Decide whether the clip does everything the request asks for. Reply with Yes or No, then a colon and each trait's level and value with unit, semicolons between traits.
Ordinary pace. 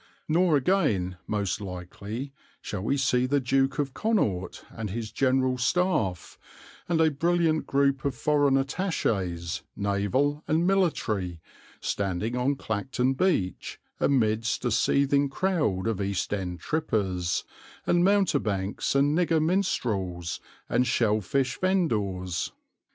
No: slow, 120 wpm